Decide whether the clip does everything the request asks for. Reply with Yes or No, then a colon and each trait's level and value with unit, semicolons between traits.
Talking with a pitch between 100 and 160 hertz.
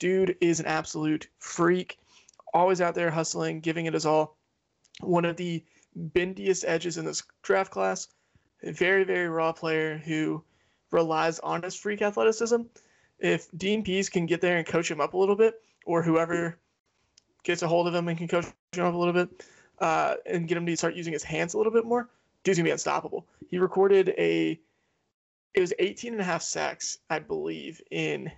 No: medium, 170 Hz